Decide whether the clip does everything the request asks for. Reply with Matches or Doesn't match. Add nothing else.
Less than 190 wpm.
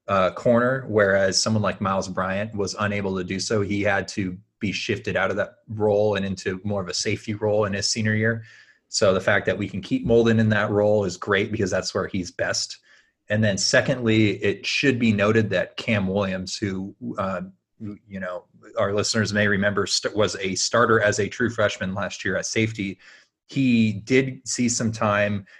Doesn't match